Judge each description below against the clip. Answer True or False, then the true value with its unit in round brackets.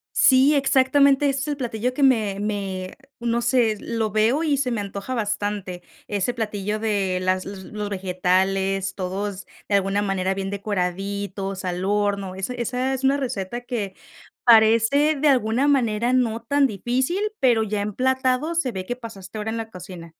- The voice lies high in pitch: True (215 Hz)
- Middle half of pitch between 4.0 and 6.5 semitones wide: True (4.5 semitones)